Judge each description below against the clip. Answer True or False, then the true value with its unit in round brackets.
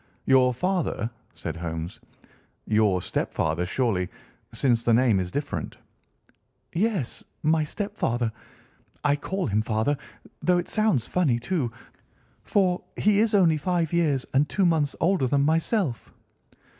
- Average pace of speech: False (130 wpm)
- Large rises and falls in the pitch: True (7.5 semitones)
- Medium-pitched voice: True (145 Hz)